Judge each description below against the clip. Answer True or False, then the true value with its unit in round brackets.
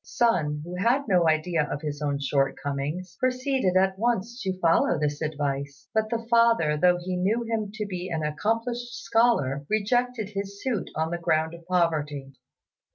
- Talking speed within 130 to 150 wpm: False (165 wpm)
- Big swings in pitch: True (7.0 semitones)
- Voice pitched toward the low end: False (180 Hz)